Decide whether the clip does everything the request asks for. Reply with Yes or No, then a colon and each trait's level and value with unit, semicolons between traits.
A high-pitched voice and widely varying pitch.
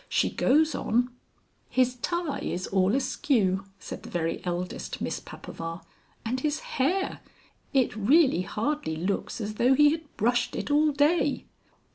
Yes: very high, 250 Hz; wide, 7.2 semitones